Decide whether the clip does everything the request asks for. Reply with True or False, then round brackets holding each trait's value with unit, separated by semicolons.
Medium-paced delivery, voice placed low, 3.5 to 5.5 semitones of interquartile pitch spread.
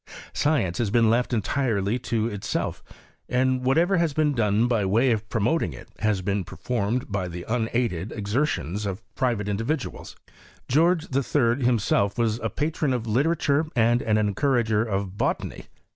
True (160 wpm; 115 Hz; 4.2 semitones)